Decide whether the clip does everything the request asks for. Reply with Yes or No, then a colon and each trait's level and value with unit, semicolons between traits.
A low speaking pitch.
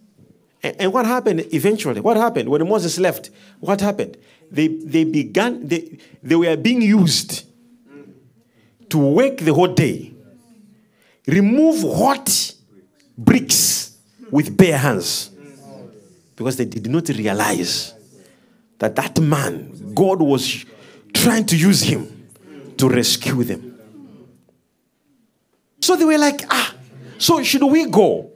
No: medium, 170 Hz